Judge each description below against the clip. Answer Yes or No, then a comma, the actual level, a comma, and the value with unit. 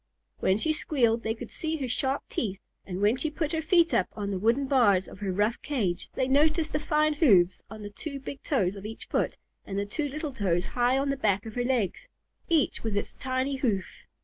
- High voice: Yes, high, 245 Hz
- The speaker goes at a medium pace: No, fast, 230 wpm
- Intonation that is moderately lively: No, wide, 6.0 semitones